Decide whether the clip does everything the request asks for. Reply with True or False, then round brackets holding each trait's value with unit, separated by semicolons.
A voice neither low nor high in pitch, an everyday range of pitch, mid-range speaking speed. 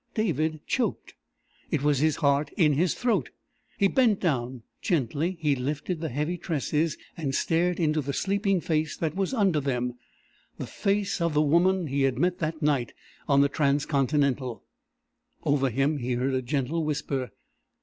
True (150 Hz; 3.8 semitones; 160 wpm)